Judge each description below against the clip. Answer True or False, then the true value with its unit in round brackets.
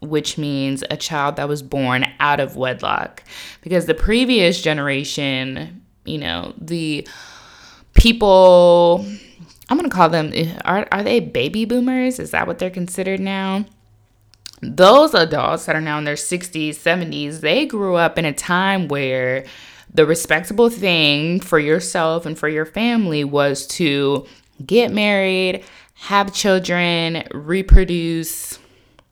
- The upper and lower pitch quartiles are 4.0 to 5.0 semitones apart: True (4.7 semitones)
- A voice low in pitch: False (165 Hz)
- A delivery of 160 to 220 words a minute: False (135 wpm)